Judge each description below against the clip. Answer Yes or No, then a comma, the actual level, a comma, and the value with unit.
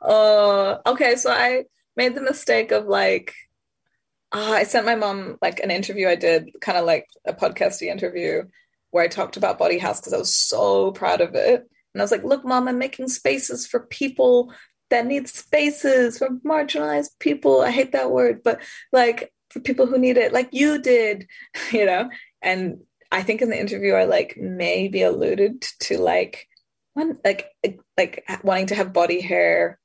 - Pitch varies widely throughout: Yes, wide, 6.6 semitones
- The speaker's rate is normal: Yes, average, 185 wpm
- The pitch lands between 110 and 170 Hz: No, high, 235 Hz